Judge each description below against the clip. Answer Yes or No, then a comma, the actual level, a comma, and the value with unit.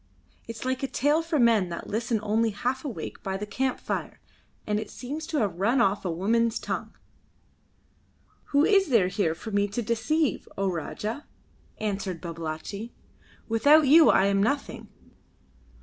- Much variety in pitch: No, average, 5.0 semitones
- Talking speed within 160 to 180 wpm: Yes, average, 165 wpm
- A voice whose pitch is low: No, high, 225 Hz